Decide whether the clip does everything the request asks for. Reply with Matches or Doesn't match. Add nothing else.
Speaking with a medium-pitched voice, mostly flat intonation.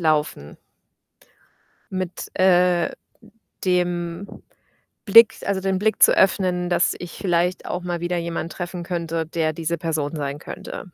Matches